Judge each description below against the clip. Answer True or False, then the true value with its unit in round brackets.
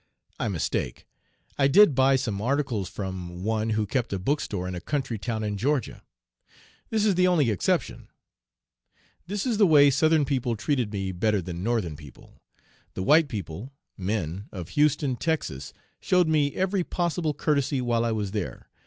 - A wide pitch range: True (7.1 semitones)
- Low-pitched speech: True (120 Hz)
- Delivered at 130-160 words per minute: False (170 wpm)